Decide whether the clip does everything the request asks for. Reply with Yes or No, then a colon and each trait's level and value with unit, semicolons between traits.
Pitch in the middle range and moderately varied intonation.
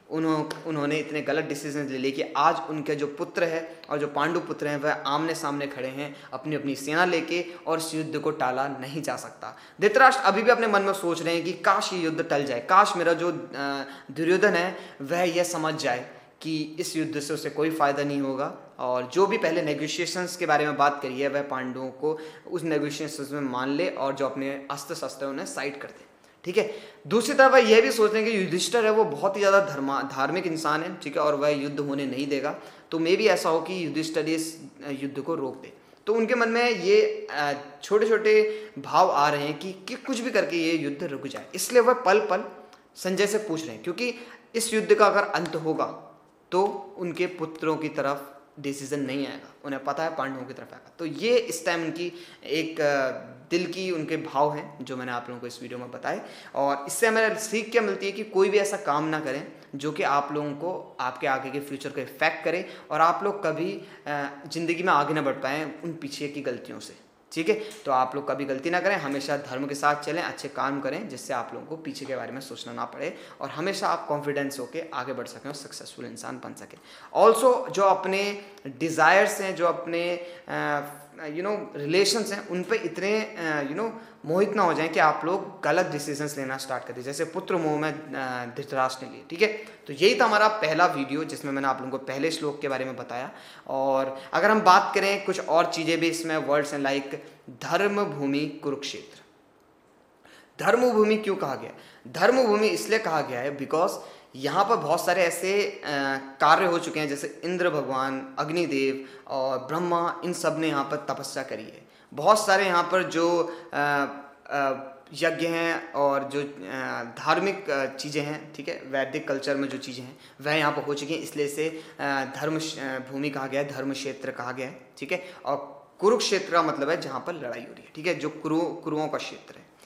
Yes: medium, 155 Hz; average, 4.3 semitones